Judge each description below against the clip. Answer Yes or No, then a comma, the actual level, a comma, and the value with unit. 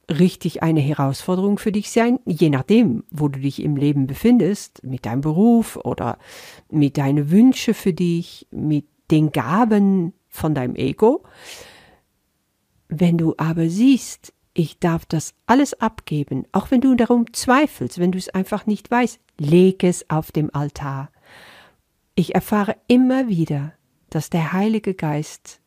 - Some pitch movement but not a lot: No, wide, 6.3 semitones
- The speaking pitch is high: No, medium, 180 Hz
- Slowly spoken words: No, average, 145 wpm